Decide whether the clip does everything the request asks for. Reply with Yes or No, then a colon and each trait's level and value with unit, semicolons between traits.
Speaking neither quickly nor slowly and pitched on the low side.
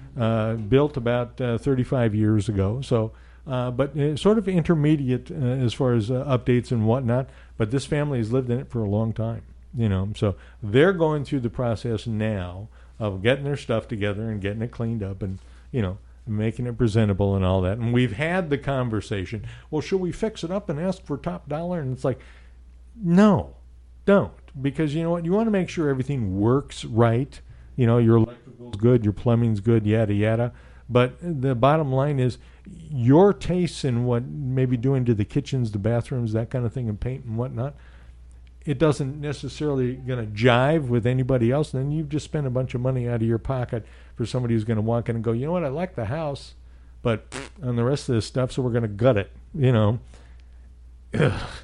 No: fast, 210 wpm; low, 120 Hz